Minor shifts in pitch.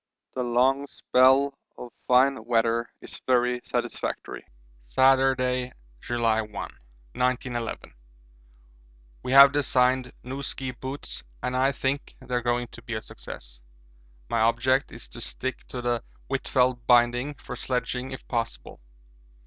Yes: narrow, 1.8 semitones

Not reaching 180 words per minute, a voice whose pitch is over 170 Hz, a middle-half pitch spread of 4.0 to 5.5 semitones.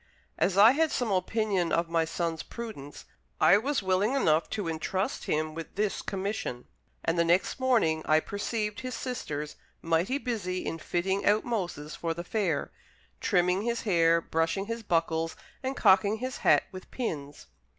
Yes: average, 160 wpm; medium, 185 Hz; average, 5.0 semitones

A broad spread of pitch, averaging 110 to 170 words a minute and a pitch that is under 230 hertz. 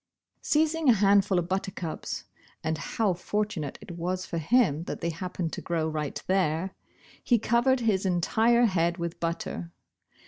No: average, 4.2 semitones; average, 150 wpm; medium, 185 Hz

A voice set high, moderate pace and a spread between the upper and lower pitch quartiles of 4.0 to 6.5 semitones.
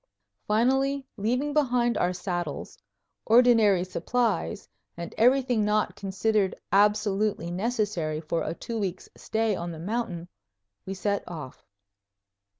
No: high, 210 Hz; slow, 115 wpm; average, 4.9 semitones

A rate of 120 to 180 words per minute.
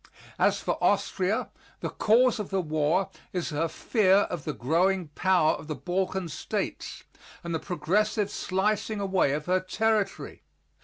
Yes: average, 150 wpm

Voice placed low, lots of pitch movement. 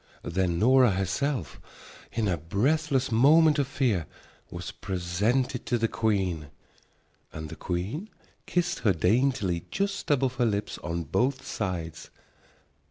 Yes: low, 110 Hz; wide, 7.2 semitones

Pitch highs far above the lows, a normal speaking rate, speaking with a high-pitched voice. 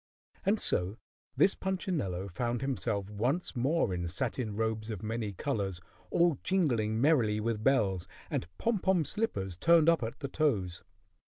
No: wide, 7.5 semitones; average, 150 wpm; low, 115 Hz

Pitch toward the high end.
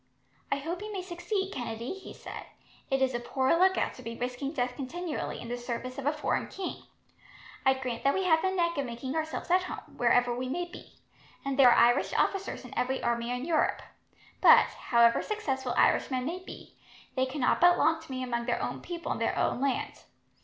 Yes: very high, 270 Hz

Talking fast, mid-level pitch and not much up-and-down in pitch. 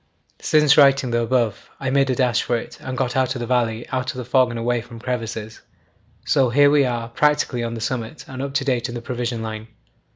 No: fast, 230 wpm; low, 125 Hz; narrow, 2.2 semitones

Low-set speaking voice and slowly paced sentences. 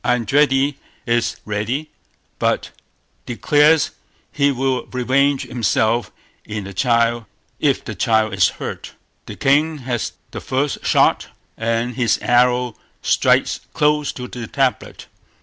Yes: low, 125 Hz; slow, 110 wpm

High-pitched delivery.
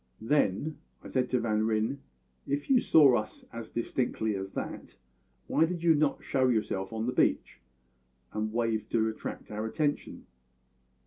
No: low, 115 Hz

